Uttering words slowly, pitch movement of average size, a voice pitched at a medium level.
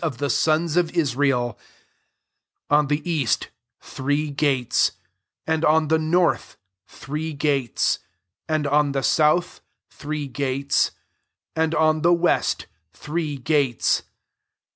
No: slow, 120 wpm; narrow, 2.2 semitones; medium, 150 Hz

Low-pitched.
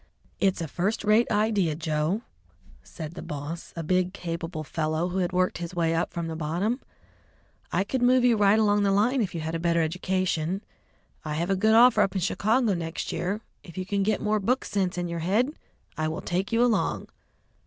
No: medium, 185 Hz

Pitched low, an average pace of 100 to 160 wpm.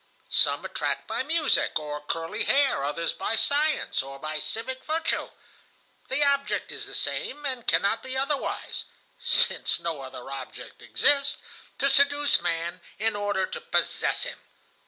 No: high, 235 Hz; average, 140 wpm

